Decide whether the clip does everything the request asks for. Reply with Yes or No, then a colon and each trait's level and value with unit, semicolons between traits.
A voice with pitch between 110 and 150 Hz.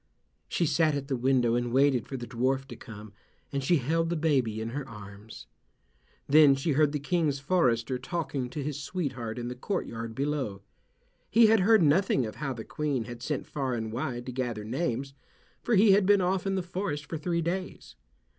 Yes: medium, 140 Hz